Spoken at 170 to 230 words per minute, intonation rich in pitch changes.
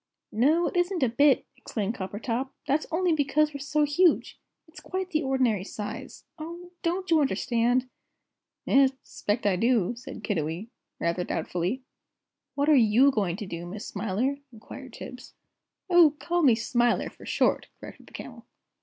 No: average, 160 wpm; wide, 6.1 semitones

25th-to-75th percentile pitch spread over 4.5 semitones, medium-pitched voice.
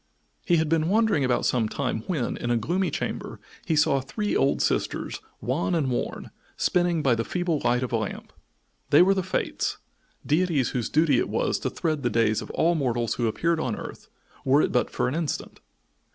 Yes: wide, 5.6 semitones; medium, 145 Hz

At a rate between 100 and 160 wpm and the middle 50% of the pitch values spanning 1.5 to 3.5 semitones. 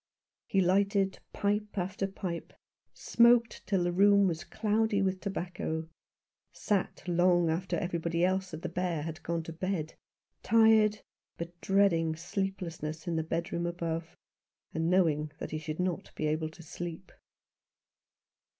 Yes: average, 140 wpm; average, 3.0 semitones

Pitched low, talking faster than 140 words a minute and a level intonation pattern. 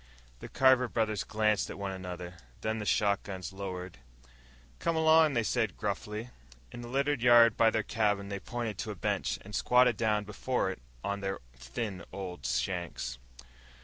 No: low, 105 Hz; average, 165 wpm; average, 3.7 semitones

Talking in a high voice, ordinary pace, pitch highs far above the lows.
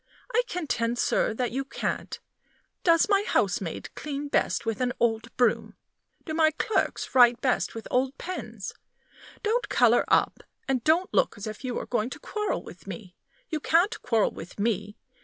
Yes: very high, 255 Hz; average, 170 wpm; wide, 6.3 semitones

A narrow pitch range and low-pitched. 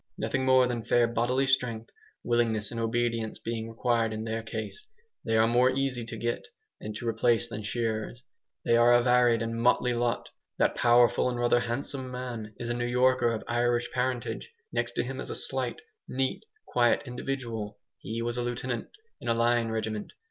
Yes: narrow, 1.4 semitones; low, 120 Hz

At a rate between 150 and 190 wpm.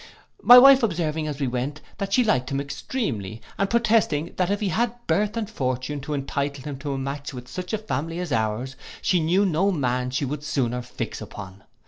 No: average, 200 wpm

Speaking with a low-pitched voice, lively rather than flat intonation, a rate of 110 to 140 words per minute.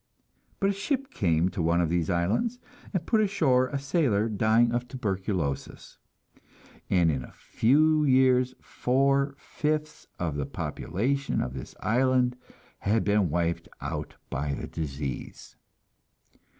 Yes: low, 120 Hz; wide, 8.2 semitones; slow, 135 wpm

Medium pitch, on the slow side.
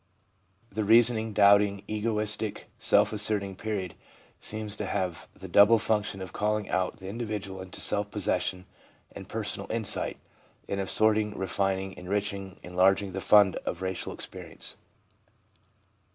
No: low, 100 Hz; slow, 130 wpm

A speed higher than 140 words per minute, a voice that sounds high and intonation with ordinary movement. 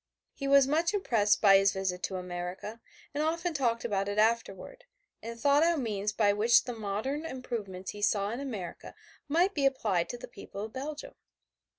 No: average, 185 wpm; high, 230 Hz; wide, 5.8 semitones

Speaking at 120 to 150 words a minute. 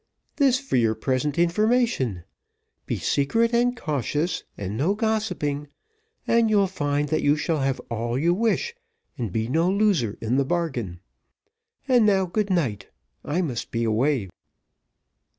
Yes: average, 145 wpm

